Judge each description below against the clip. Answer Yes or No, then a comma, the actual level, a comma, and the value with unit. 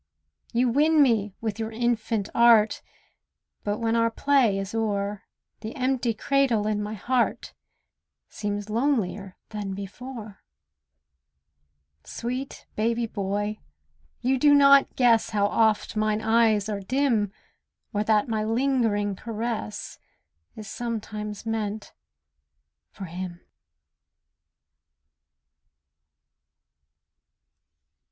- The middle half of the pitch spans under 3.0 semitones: Yes, narrow, 2.6 semitones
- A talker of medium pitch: No, high, 220 Hz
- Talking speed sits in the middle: No, slow, 100 wpm